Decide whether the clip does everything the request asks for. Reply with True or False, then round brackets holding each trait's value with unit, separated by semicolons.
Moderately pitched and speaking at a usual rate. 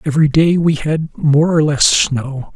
True (150 Hz; 190 wpm)